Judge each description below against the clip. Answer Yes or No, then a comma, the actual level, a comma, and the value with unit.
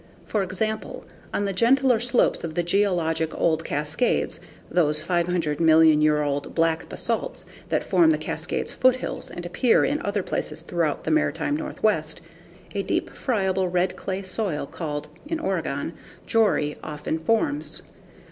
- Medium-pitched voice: Yes, medium, 180 Hz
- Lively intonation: Yes, wide, 6.1 semitones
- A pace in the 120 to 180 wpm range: Yes, average, 145 wpm